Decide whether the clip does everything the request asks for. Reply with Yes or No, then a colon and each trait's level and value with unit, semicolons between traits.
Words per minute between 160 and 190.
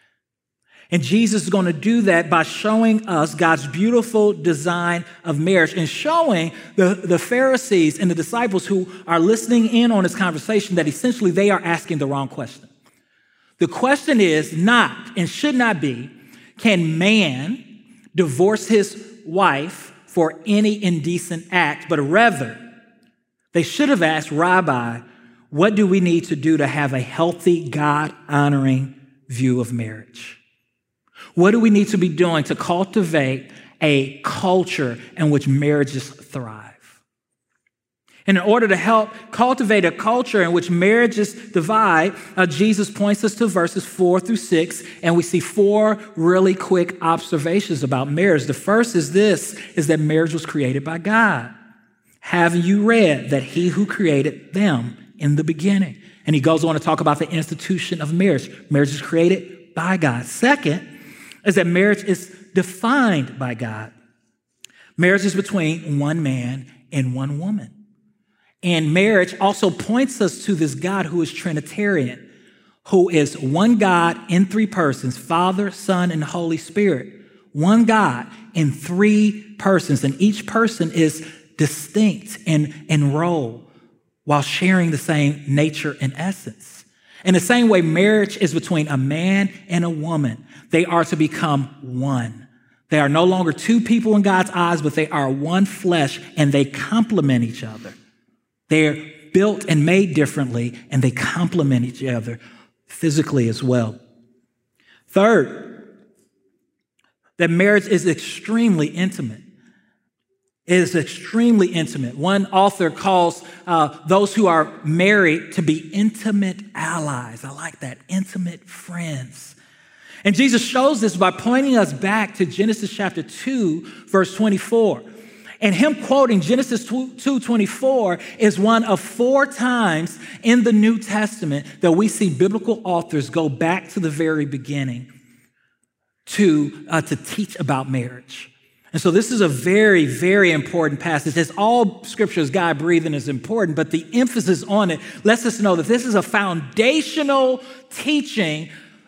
No: average, 150 wpm